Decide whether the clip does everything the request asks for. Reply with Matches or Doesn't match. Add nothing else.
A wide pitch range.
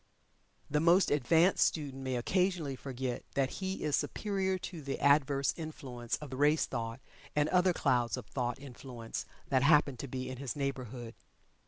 Doesn't match